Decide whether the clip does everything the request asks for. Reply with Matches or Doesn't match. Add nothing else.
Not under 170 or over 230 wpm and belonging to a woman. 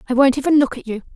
Doesn't match